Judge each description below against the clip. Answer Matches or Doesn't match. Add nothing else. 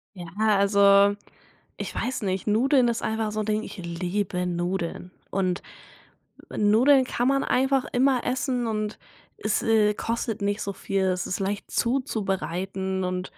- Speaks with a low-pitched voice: Doesn't match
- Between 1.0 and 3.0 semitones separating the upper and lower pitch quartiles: Doesn't match